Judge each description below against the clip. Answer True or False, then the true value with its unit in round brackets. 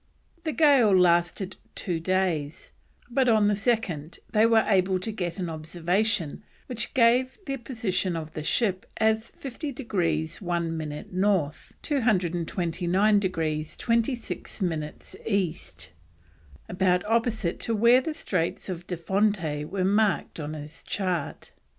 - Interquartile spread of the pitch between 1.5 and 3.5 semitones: False (4.9 semitones)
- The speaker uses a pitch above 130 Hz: True (190 Hz)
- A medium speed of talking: False (130 wpm)